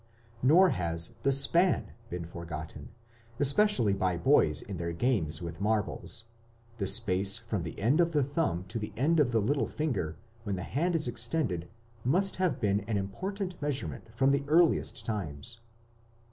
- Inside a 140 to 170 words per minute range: Yes, average, 160 wpm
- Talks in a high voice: No, low, 115 Hz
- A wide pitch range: Yes, wide, 8.4 semitones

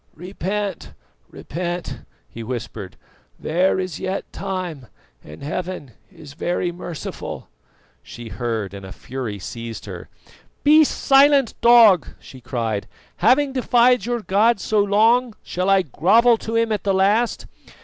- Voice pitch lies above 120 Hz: Yes, medium, 185 Hz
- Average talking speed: No, slow, 130 wpm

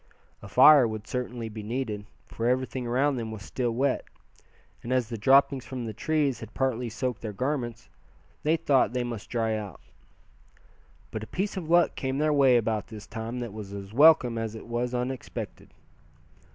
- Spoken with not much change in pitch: No, average, 3.0 semitones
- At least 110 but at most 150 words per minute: No, average, 180 wpm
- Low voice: Yes, low, 120 Hz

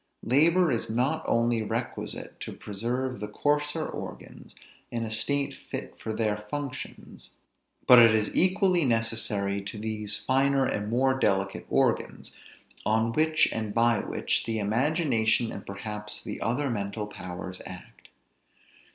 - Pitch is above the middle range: No, low, 115 Hz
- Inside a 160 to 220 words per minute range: No, slow, 135 wpm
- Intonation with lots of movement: No, average, 4.4 semitones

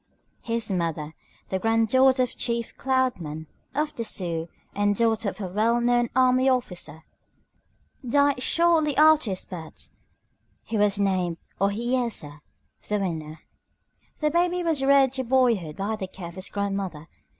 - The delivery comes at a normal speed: Yes, average, 145 wpm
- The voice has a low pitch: No, high, 225 Hz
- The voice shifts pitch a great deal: Yes, wide, 5.7 semitones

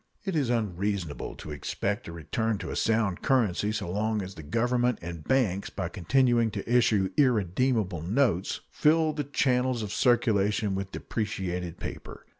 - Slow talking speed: No, average, 155 wpm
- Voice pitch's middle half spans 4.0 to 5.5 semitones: Yes, average, 4.6 semitones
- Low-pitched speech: Yes, low, 105 Hz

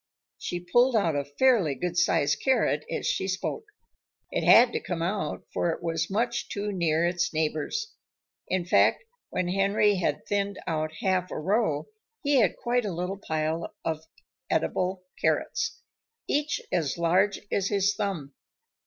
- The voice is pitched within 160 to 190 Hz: Yes, medium, 185 Hz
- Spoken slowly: No, average, 155 wpm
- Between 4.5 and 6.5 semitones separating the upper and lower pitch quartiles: No, average, 4.0 semitones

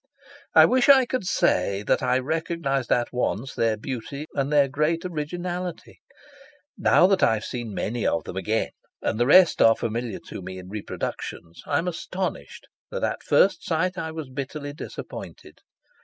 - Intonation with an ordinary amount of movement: No, wide, 7.2 semitones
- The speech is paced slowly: No, average, 170 wpm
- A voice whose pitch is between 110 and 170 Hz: Yes, medium, 140 Hz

